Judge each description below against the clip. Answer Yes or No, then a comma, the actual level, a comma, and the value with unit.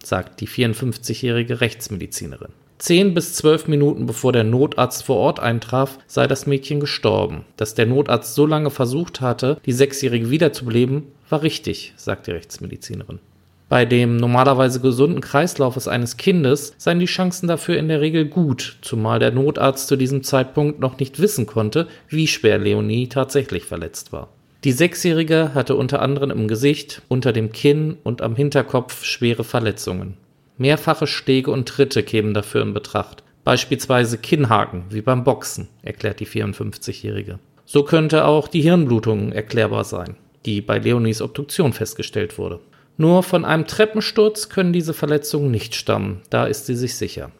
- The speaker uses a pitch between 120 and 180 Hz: Yes, low, 135 Hz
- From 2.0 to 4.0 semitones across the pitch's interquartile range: No, average, 4.6 semitones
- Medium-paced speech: Yes, average, 155 wpm